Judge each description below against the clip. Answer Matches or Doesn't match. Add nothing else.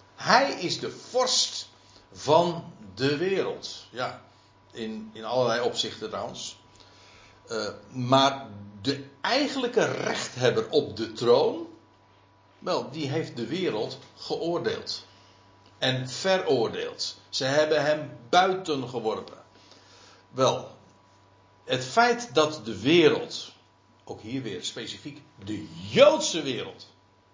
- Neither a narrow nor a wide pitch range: Doesn't match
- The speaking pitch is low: Matches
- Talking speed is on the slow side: Matches